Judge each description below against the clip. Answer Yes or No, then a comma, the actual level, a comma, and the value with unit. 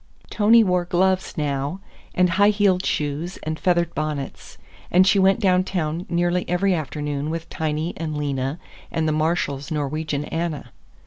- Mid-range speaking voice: Yes, medium, 165 Hz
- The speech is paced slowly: No, average, 145 wpm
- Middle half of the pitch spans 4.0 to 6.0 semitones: No, average, 3.4 semitones